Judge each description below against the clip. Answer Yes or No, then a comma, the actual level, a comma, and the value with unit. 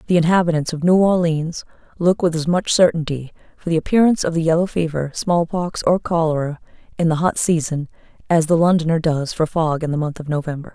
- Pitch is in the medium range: Yes, medium, 165 Hz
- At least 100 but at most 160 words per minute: No, average, 200 wpm